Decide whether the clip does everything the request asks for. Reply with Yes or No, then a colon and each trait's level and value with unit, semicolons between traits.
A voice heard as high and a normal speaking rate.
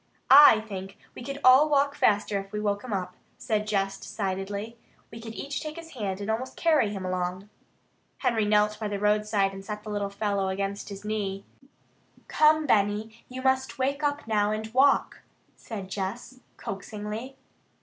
Yes: high, 210 Hz; average, 170 wpm